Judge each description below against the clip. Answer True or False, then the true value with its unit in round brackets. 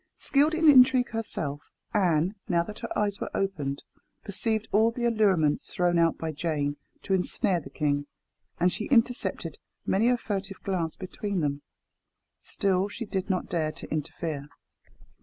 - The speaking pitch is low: False (190 Hz)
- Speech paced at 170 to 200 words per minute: False (155 wpm)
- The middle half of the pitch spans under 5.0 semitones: False (5.4 semitones)